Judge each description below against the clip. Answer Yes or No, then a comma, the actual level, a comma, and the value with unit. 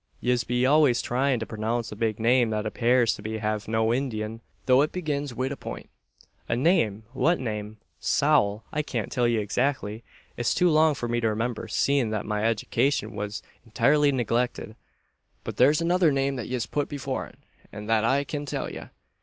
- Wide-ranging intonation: No, average, 4.1 semitones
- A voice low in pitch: Yes, low, 120 Hz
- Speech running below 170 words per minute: No, average, 185 wpm